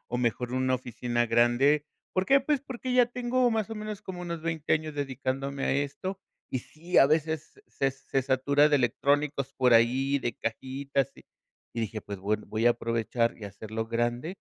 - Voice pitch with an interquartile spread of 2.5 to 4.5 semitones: No, average, 5.1 semitones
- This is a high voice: No, low, 135 Hz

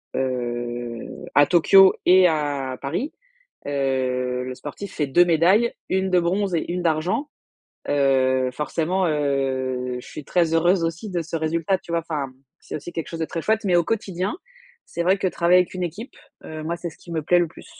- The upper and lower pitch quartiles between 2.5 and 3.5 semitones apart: No, average, 4.8 semitones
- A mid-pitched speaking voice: Yes, medium, 165 Hz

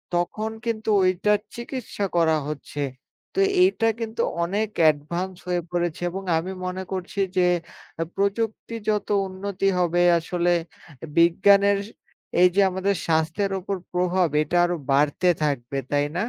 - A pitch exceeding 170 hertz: Yes, medium, 185 Hz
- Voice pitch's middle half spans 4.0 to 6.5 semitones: No, average, 2.9 semitones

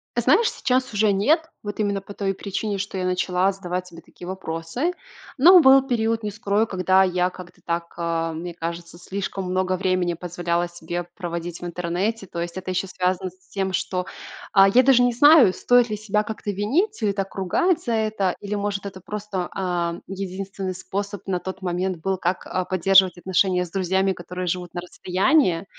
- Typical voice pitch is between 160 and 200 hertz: Yes, high, 190 Hz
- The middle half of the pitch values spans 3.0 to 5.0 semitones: No, narrow, 2.6 semitones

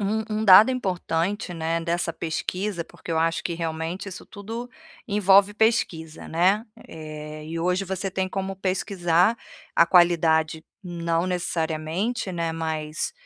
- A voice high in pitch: No, medium, 175 Hz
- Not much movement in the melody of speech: No, average, 3.2 semitones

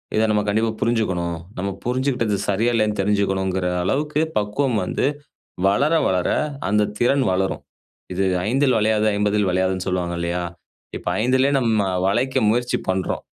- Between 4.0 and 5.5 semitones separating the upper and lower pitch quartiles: Yes, average, 4.3 semitones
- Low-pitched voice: Yes, low, 105 Hz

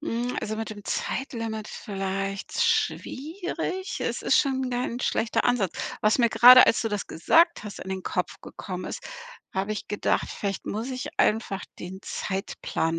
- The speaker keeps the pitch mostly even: No, average, 4.3 semitones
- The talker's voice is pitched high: Yes, high, 220 Hz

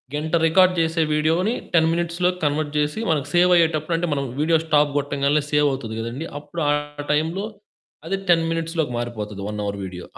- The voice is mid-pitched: Yes, medium, 155 Hz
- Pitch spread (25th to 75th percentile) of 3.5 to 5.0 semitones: No, average, 2.8 semitones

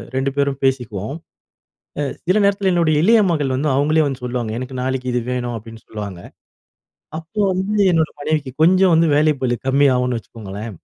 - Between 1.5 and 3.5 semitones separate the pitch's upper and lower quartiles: No, average, 4.7 semitones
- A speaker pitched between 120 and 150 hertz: Yes, low, 135 Hz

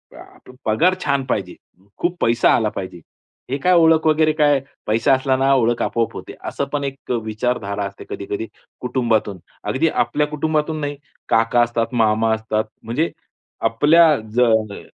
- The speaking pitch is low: Yes, low, 125 Hz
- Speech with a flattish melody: No, average, 4.8 semitones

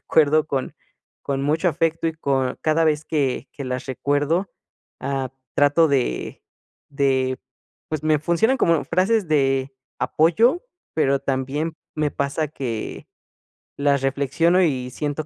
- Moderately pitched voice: Yes, medium, 145 Hz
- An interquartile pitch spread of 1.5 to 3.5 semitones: Yes, average, 3.0 semitones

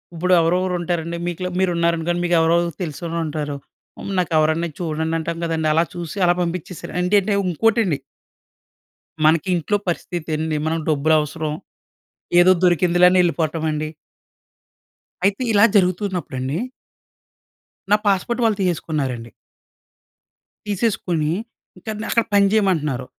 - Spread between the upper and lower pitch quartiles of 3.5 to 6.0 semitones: No, average, 2.7 semitones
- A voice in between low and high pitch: Yes, medium, 170 Hz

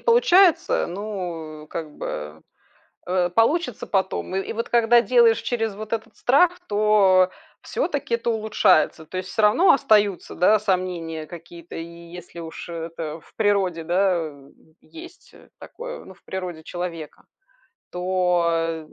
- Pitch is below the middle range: No, medium, 185 Hz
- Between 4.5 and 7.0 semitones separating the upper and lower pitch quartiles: Yes, average, 5.1 semitones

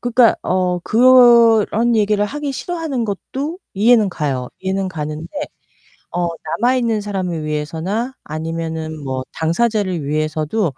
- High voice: Yes, high, 195 Hz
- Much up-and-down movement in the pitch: Yes, wide, 6.8 semitones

